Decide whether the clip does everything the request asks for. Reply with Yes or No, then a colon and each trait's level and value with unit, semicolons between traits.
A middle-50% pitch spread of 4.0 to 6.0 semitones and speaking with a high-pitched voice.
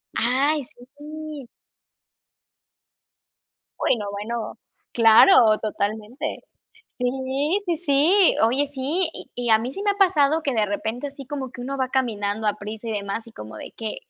Yes: average, 4.9 semitones; very high, 250 Hz